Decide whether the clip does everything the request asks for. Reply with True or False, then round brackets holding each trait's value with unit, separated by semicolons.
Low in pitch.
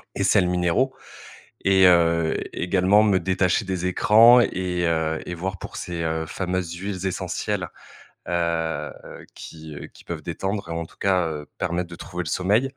True (90 Hz)